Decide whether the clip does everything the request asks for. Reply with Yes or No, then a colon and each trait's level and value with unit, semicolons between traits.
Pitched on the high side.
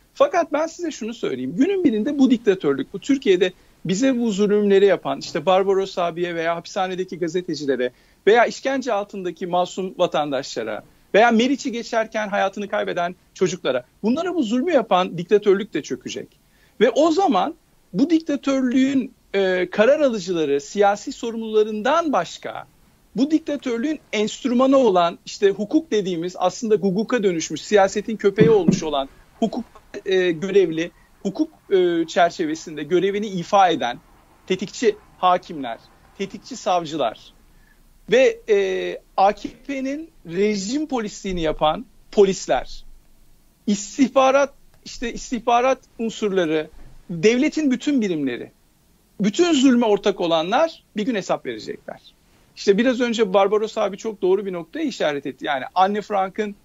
Yes: high, 210 Hz